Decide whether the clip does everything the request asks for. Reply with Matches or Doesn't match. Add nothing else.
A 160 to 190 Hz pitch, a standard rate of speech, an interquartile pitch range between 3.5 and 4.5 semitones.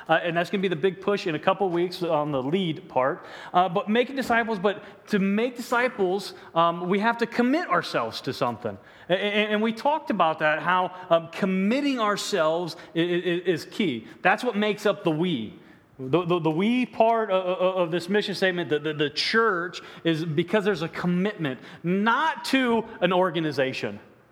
Matches